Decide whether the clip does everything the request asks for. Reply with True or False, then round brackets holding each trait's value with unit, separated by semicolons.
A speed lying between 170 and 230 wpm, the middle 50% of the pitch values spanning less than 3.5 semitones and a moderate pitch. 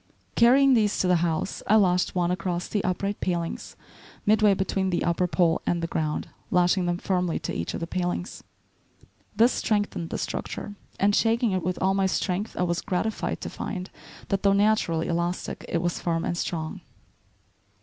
True (180 wpm; 2.8 semitones; 180 Hz)